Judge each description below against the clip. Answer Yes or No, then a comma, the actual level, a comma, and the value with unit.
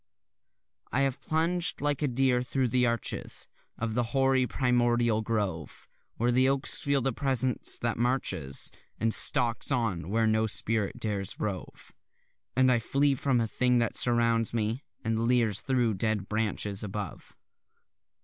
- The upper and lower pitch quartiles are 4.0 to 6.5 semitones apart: No, average, 3.0 semitones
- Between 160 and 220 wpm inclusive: No, average, 150 wpm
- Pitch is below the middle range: Yes, low, 120 Hz